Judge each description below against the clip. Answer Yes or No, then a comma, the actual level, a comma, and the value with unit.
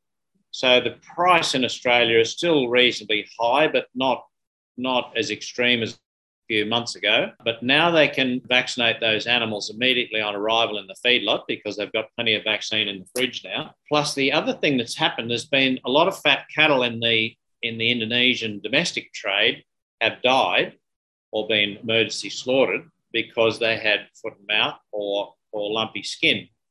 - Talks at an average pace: Yes, average, 175 wpm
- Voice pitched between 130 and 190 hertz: No, low, 115 Hz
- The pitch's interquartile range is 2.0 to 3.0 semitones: Yes, average, 2.7 semitones